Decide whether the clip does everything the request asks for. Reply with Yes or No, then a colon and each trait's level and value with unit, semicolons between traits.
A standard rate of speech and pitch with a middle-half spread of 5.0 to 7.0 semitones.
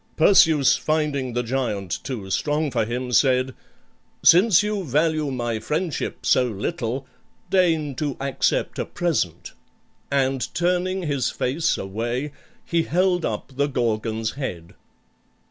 No: slow, 125 wpm; average, 5.3 semitones